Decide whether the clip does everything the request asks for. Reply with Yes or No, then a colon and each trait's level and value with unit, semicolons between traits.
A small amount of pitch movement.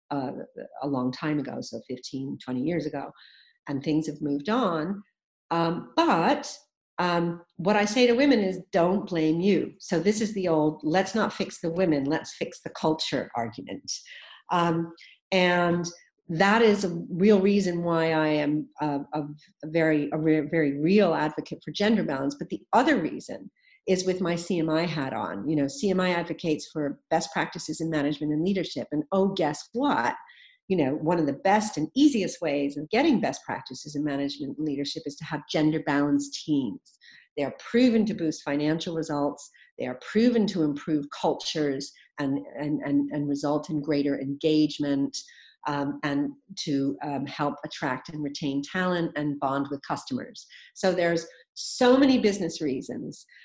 No: average, 4.7 semitones